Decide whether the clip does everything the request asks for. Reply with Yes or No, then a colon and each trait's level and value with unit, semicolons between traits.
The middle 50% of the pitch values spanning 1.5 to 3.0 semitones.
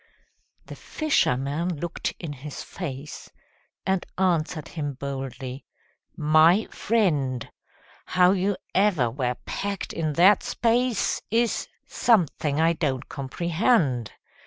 No: wide, 5.6 semitones